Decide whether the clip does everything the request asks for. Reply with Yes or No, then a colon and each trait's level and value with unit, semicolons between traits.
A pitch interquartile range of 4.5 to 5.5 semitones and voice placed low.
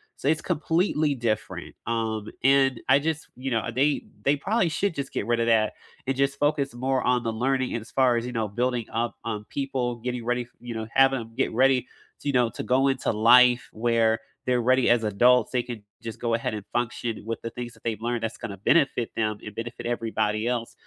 No: average, 2.7 semitones; low, 120 Hz